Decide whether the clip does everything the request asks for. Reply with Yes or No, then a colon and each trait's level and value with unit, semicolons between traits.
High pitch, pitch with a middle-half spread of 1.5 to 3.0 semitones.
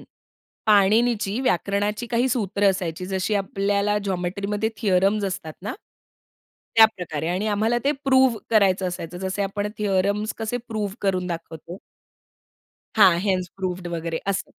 Yes: high, 200 Hz; average, 2.7 semitones